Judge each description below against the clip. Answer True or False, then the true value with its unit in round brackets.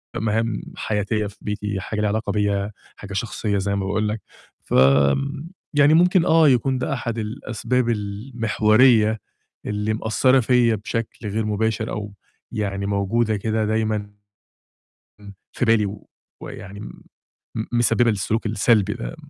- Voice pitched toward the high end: False (110 Hz)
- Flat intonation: True (2.2 semitones)